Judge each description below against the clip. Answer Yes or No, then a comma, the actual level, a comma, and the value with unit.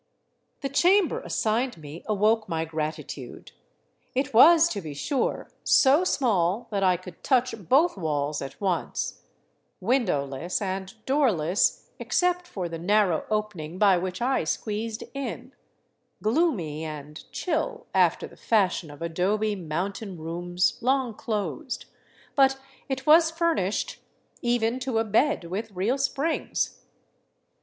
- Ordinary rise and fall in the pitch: No, wide, 7.3 semitones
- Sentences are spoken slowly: Yes, slow, 125 wpm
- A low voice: No, high, 210 Hz